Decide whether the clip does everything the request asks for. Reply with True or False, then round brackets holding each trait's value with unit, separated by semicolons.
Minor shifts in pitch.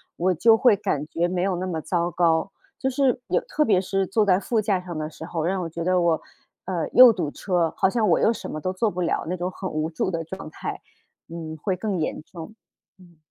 False (3.0 semitones)